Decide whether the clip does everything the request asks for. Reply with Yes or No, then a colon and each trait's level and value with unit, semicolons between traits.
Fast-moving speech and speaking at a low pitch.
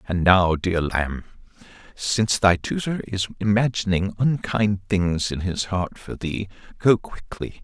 No: average, 140 wpm; very low, 95 Hz